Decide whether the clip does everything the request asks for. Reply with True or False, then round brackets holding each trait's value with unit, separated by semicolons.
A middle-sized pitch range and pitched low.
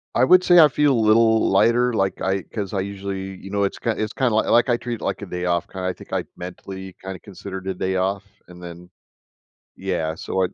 True (3.1 semitones; 95 Hz)